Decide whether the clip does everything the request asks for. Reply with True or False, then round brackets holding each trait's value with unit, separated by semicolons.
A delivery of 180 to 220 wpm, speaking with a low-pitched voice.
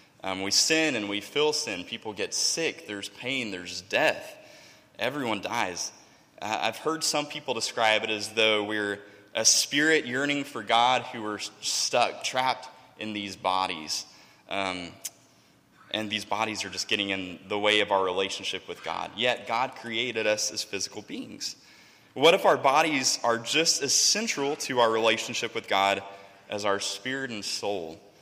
False (165 wpm; 105 Hz)